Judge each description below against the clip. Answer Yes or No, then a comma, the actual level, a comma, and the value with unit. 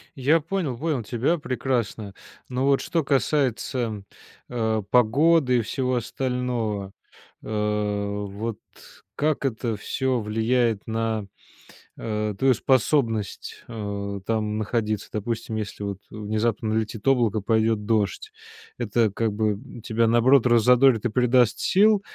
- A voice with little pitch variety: No, average, 3.1 semitones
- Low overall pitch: Yes, low, 115 Hz